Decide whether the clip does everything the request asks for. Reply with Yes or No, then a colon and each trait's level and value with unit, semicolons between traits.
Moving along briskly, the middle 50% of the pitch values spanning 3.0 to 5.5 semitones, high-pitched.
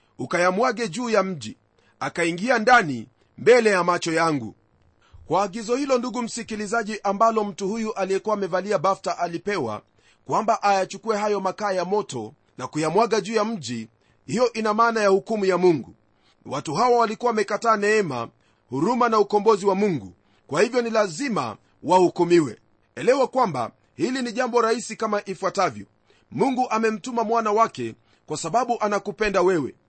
Yes: fast, 145 wpm; average, 4.6 semitones; high, 205 Hz